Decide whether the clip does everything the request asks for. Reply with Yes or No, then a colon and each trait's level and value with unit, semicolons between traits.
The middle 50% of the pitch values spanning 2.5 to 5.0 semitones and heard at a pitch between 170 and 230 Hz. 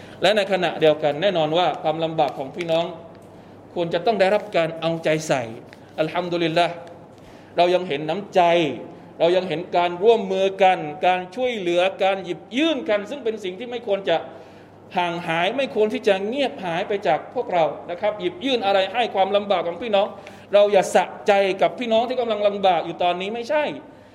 Yes: average, 3.4 semitones; medium, 185 Hz